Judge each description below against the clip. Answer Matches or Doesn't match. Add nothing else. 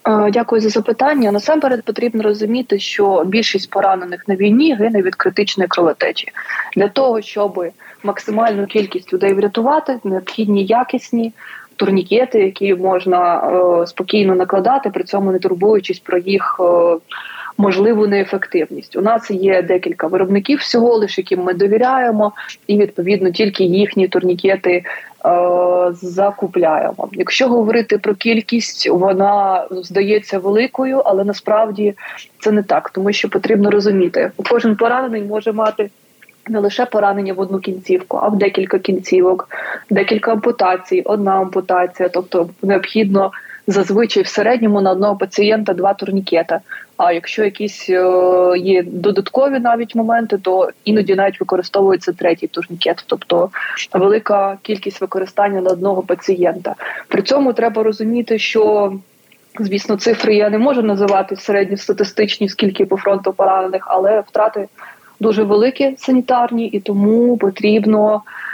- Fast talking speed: Doesn't match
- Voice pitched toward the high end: Matches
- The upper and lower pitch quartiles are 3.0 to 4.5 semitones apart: Doesn't match